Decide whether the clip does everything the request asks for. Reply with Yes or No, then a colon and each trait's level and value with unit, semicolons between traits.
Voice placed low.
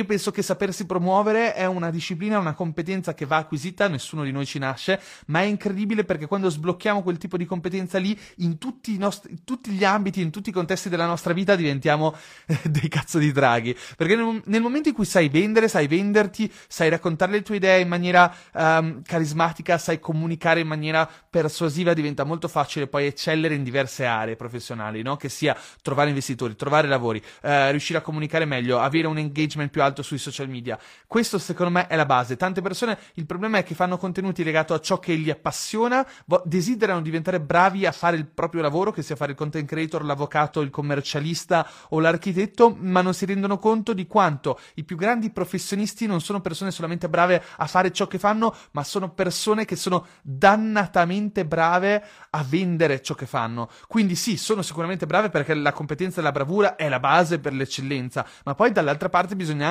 No: medium, 170 Hz